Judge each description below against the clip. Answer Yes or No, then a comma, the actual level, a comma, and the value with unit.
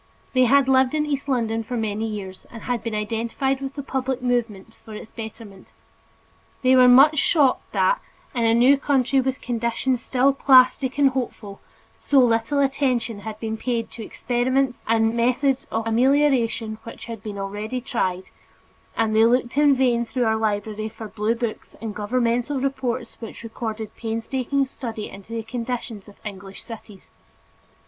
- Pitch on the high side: Yes, high, 235 Hz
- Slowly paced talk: No, average, 165 wpm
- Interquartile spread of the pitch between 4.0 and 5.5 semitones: No, average, 3.0 semitones